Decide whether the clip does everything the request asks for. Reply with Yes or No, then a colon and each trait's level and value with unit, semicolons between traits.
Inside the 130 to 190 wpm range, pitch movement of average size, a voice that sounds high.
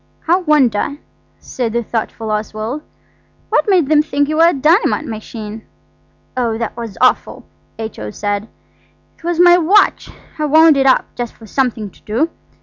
No: average, 160 wpm; wide, 6.0 semitones; very high, 255 Hz